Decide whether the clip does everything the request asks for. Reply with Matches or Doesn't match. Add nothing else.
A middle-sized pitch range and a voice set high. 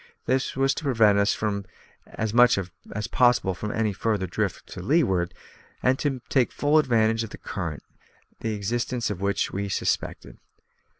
Doesn't match